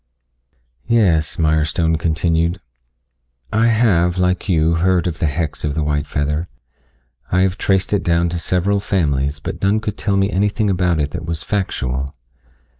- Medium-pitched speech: No, very low, 85 Hz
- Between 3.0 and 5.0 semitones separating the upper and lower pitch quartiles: Yes, average, 3.8 semitones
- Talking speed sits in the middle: Yes, average, 160 wpm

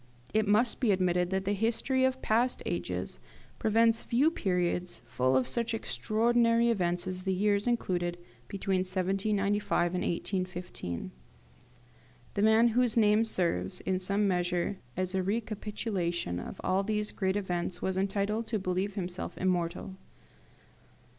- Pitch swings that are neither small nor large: Yes, average, 3.4 semitones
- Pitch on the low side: No, high, 195 Hz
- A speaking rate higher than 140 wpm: No, slow, 135 wpm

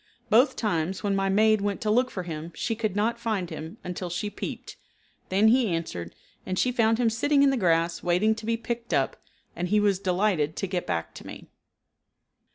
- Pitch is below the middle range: No, high, 200 Hz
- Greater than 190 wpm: Yes, fast, 205 wpm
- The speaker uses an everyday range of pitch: Yes, average, 4.2 semitones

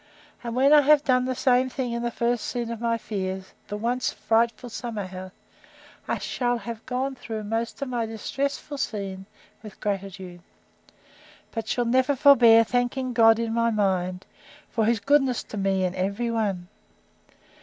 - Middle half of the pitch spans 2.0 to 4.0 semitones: Yes, average, 3.3 semitones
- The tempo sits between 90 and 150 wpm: No, average, 165 wpm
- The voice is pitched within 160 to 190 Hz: No, high, 230 Hz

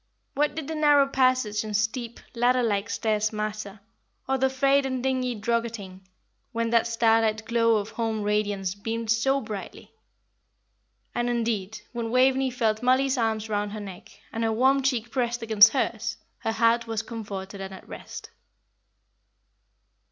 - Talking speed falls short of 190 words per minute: Yes, average, 150 wpm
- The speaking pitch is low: No, high, 230 Hz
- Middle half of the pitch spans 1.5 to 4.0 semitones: Yes, average, 3.0 semitones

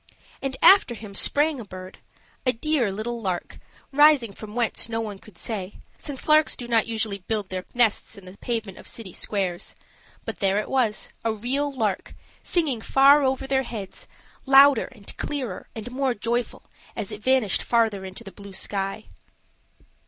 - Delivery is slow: No, average, 170 wpm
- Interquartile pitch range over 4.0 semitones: Yes, average, 4.7 semitones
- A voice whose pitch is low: No, high, 225 Hz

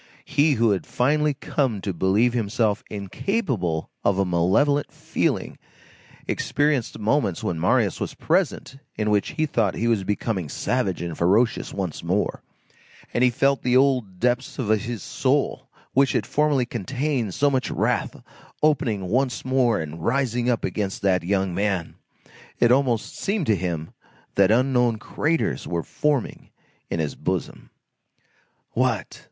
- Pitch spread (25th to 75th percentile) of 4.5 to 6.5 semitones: Yes, wide, 5.6 semitones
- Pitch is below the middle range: Yes, low, 115 Hz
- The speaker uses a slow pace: No, average, 145 wpm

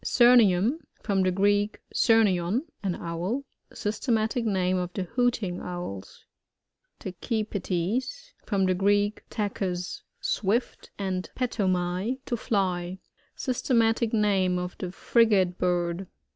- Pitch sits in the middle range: No, high, 195 Hz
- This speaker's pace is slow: Yes, slow, 115 wpm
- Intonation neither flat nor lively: Yes, average, 3.8 semitones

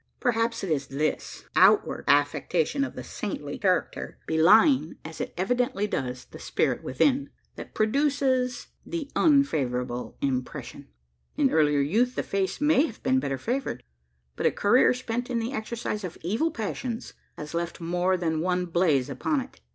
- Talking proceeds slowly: No, average, 155 wpm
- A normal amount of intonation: No, wide, 8.4 semitones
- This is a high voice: Yes, high, 200 Hz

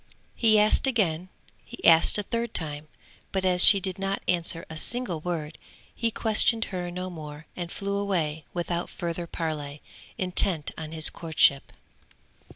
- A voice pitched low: No, medium, 175 Hz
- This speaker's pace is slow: No, average, 155 wpm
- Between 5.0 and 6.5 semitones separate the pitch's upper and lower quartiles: No, average, 3.8 semitones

